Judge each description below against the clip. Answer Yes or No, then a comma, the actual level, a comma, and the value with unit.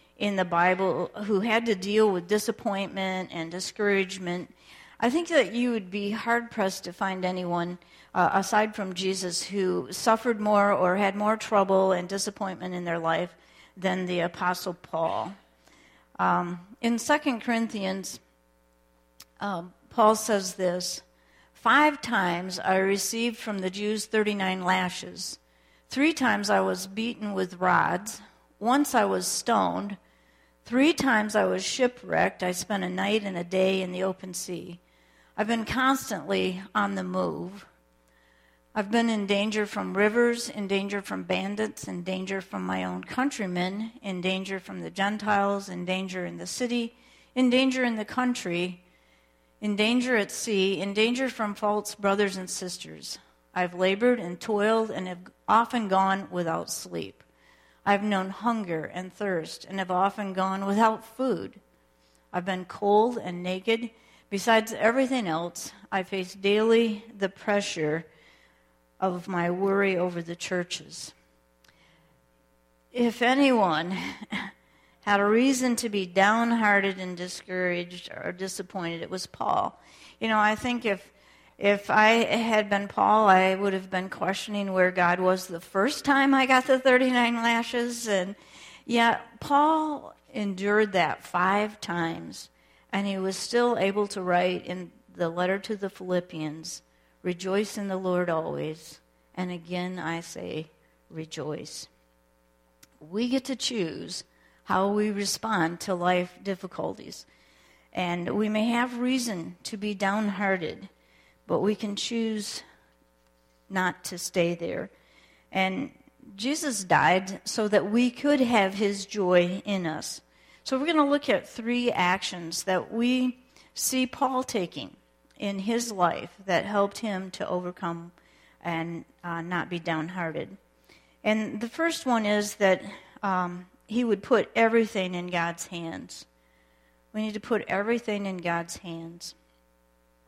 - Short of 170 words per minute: Yes, average, 140 wpm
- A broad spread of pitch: No, average, 3.7 semitones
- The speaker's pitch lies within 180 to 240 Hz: Yes, high, 190 Hz